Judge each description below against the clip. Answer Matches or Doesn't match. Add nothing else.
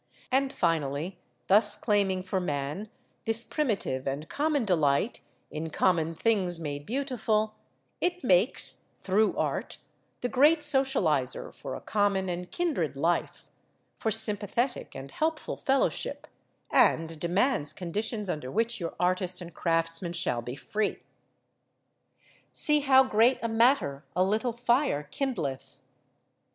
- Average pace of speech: Doesn't match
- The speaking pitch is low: Doesn't match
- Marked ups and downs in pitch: Matches